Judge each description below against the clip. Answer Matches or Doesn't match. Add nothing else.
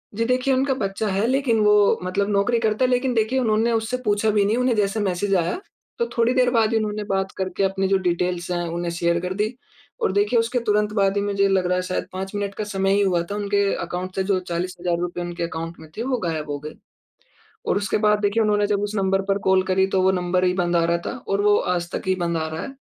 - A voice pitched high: Matches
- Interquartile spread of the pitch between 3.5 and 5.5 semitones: Doesn't match